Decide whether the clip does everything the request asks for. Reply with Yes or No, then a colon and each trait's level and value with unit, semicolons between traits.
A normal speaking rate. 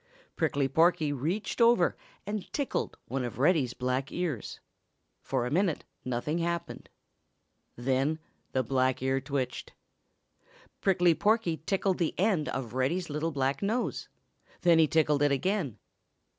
No: slow, 130 wpm